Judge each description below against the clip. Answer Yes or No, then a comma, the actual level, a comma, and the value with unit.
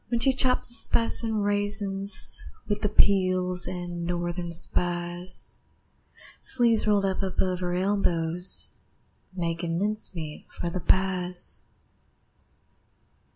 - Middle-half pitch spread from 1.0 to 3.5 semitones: Yes, average, 2.7 semitones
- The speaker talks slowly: Yes, slow, 110 wpm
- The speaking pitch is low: No, medium, 185 Hz